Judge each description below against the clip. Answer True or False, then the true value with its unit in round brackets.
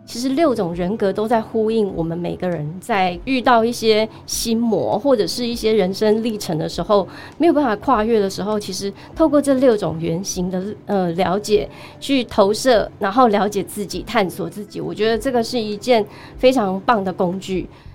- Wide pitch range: False (4.1 semitones)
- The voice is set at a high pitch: True (210 Hz)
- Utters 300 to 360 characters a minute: False (275 characters per minute)